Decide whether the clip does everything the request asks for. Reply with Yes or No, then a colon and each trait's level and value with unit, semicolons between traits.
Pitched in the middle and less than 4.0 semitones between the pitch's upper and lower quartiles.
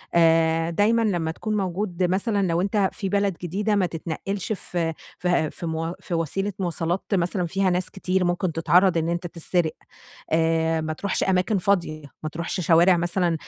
Yes: medium, 175 Hz; average, 2.9 semitones